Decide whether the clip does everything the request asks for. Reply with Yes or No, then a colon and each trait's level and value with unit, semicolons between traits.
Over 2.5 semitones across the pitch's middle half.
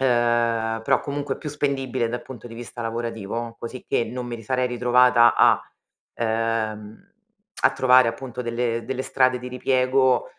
No: narrow, 1.8 semitones